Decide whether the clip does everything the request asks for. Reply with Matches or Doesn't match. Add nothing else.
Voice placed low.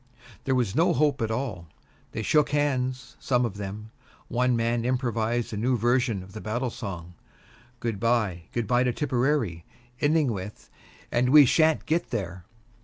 Matches